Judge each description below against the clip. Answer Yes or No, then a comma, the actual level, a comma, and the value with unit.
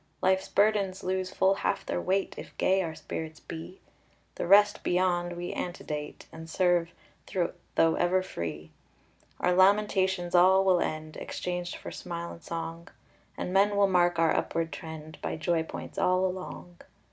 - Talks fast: No, average, 155 wpm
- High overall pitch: No, medium, 180 Hz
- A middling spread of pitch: No, narrow, 2.3 semitones